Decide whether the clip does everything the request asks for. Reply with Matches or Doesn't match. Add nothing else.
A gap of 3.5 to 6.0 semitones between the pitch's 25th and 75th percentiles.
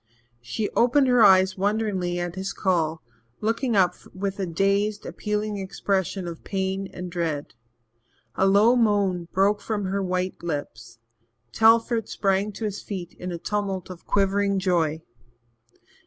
Doesn't match